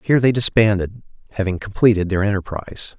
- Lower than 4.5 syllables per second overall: No, 6.3 syllables/s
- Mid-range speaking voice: No, low, 100 Hz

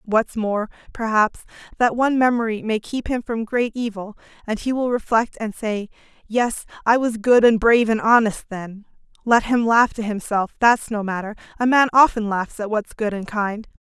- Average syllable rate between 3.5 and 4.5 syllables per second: No, 4.9 syllables/s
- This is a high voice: Yes, high, 220 Hz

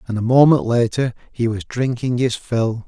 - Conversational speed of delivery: Yes, average, 190 wpm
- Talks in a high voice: No, low, 120 Hz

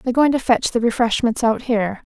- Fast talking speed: Yes, fast, 230 wpm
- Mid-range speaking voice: No, high, 235 Hz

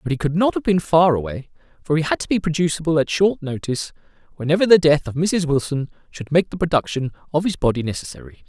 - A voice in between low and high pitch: Yes, medium, 155 Hz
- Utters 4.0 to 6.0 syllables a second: No, 6.3 syllables/s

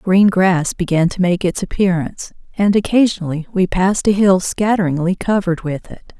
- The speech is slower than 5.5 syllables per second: Yes, 5.3 syllables/s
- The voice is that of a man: No, female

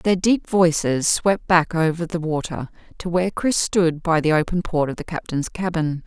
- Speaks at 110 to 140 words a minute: No, average, 200 wpm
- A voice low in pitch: No, medium, 170 Hz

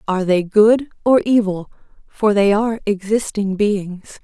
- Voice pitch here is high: Yes, high, 205 Hz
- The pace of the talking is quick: No, average, 140 wpm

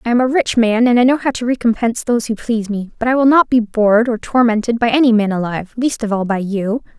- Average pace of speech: No, fast, 265 wpm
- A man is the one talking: No, female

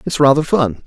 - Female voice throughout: No, male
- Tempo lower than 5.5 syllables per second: Yes, 5.3 syllables/s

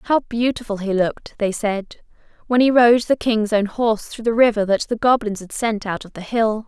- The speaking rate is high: Yes, fast, 225 wpm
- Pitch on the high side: Yes, high, 220 Hz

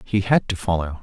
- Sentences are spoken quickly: Yes, fast, 235 wpm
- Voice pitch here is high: No, low, 100 Hz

